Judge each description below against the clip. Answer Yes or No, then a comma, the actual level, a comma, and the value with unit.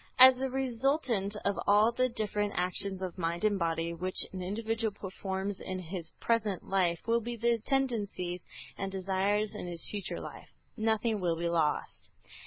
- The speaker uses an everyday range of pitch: Yes, average, 3.9 semitones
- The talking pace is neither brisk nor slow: Yes, average, 165 wpm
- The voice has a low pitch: No, high, 200 Hz